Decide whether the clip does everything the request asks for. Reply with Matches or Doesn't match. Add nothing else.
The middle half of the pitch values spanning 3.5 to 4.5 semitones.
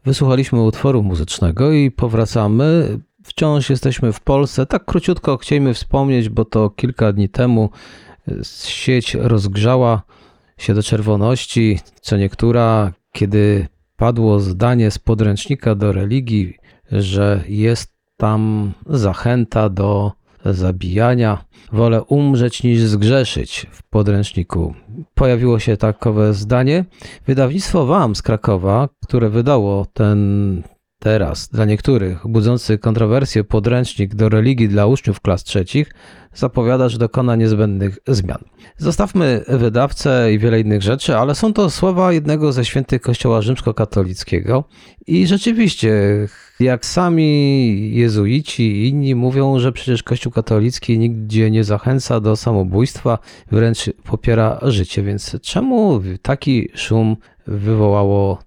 Matches